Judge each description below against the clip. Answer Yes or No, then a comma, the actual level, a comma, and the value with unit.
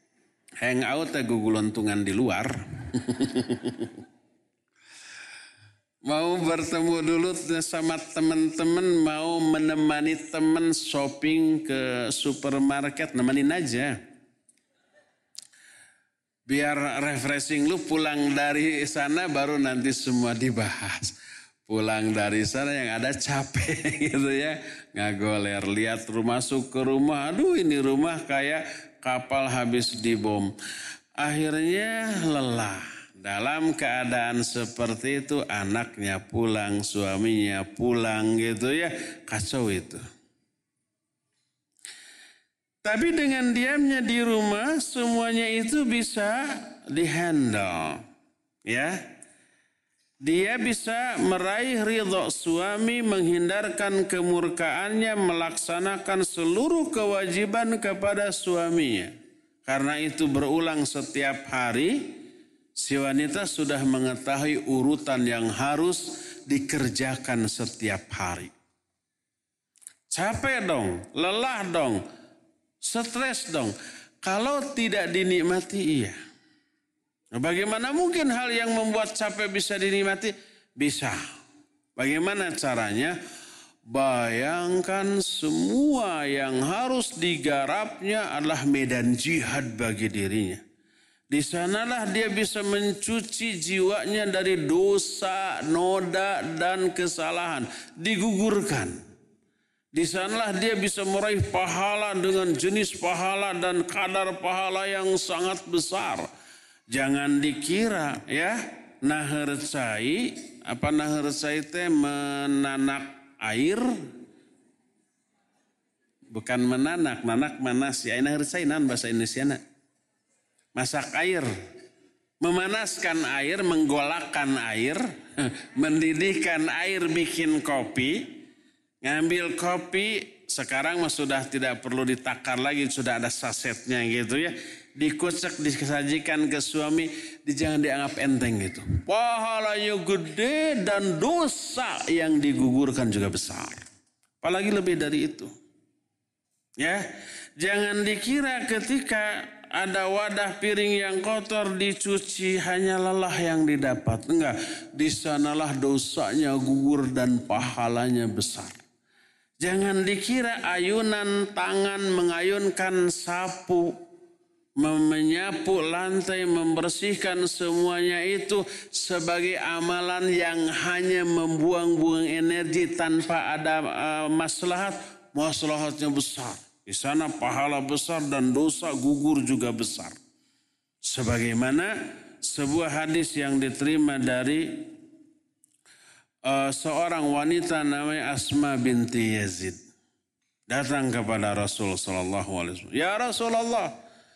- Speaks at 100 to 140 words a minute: No, average, 90 wpm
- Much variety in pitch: Yes, wide, 7.4 semitones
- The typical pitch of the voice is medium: Yes, medium, 170 Hz